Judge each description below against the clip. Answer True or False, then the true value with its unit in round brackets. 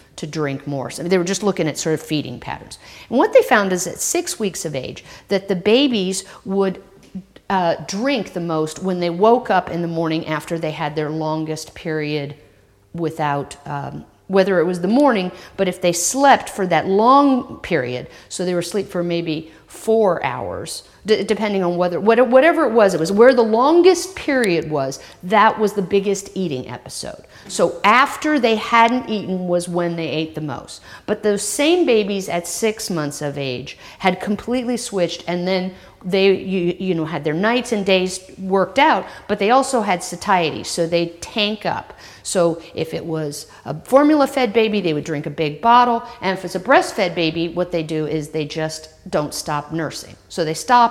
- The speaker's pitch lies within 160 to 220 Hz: True (185 Hz)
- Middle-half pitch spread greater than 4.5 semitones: True (5.1 semitones)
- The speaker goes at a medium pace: True (195 wpm)